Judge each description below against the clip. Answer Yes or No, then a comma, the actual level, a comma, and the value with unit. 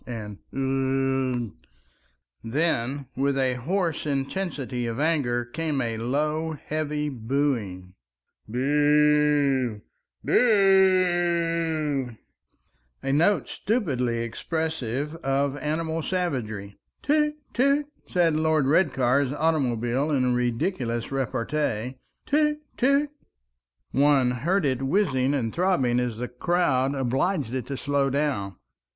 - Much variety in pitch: No, average, 4.6 semitones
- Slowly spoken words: Yes, slow, 100 wpm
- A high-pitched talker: No, medium, 140 Hz